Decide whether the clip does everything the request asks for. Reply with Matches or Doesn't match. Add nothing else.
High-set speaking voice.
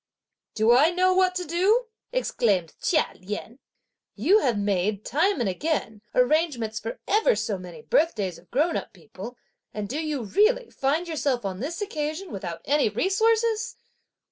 Matches